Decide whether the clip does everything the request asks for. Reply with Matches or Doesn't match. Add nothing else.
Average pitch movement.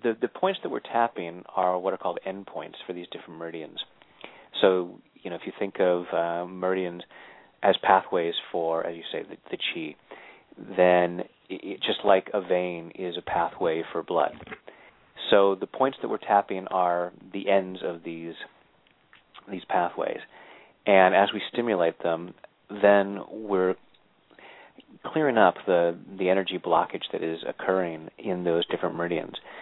Doesn't match